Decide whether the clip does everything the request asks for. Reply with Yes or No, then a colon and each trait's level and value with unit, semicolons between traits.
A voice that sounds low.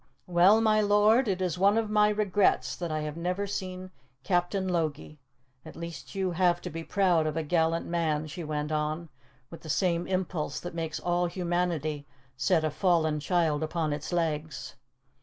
No: medium, 170 Hz